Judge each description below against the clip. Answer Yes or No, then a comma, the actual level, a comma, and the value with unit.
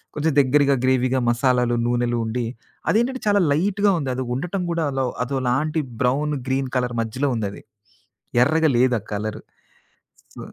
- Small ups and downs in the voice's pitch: No, average, 3.7 semitones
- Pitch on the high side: No, low, 130 Hz